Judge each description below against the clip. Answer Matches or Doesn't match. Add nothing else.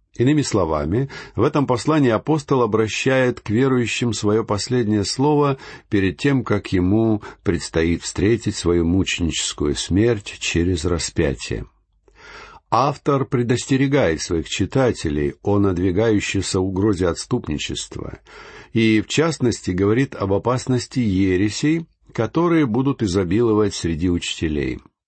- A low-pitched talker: Matches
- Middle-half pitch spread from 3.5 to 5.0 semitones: Doesn't match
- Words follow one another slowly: Matches